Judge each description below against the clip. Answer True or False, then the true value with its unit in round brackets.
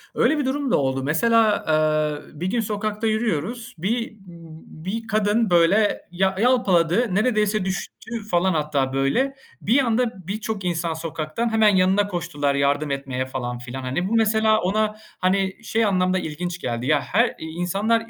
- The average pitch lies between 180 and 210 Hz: True (190 Hz)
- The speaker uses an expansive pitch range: True (6.1 semitones)